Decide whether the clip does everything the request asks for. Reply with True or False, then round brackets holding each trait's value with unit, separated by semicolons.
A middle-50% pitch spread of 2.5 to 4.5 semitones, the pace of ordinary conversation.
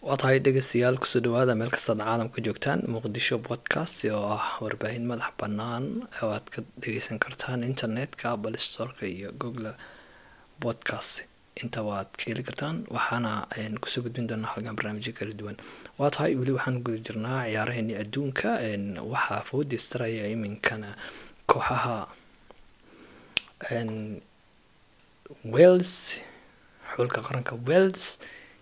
False (3.1 semitones; 120 wpm)